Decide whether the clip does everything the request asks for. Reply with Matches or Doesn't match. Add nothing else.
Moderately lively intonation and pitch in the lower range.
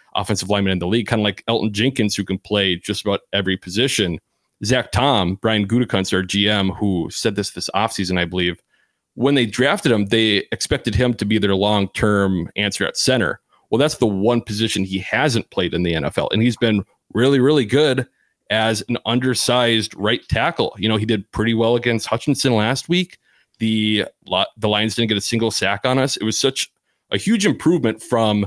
Matches